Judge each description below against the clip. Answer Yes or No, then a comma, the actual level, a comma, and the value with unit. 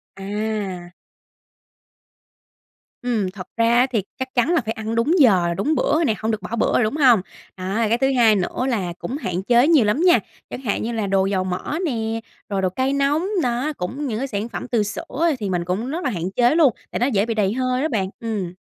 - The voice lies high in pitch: Yes, high, 225 Hz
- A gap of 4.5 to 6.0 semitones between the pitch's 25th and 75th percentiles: Yes, average, 4.8 semitones